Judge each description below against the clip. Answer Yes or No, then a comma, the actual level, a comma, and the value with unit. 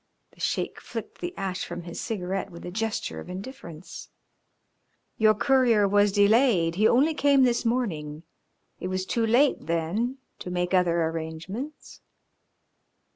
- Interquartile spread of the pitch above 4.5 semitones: Yes, wide, 5.4 semitones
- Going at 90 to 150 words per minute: Yes, average, 140 wpm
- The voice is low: No, high, 195 Hz